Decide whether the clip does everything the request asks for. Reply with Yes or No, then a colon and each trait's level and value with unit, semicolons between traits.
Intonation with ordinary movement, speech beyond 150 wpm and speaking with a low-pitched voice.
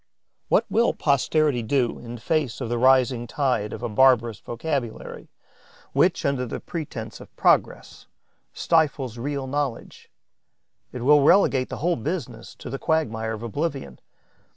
No: average, 3.9 semitones; average, 140 wpm; low, 130 Hz